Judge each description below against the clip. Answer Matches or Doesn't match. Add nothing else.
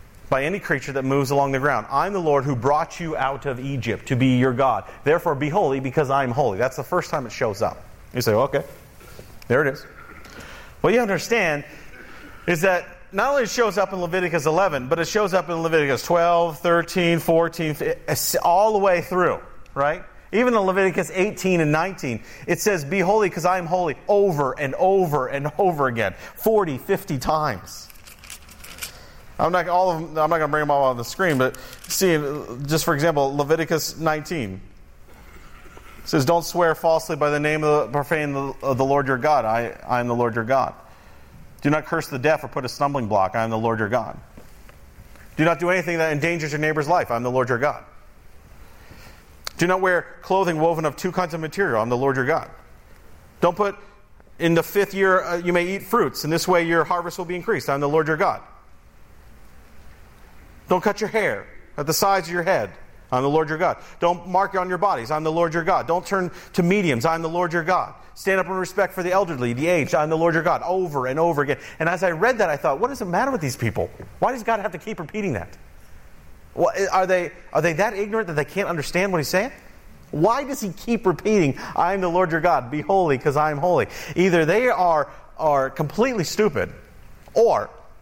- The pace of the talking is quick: Matches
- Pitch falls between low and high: Matches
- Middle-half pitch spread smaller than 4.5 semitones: Doesn't match